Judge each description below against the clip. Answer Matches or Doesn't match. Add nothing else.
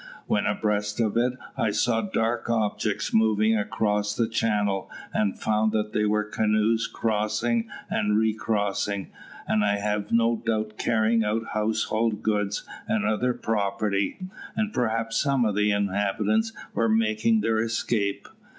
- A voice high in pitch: Doesn't match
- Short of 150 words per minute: Matches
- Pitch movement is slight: Matches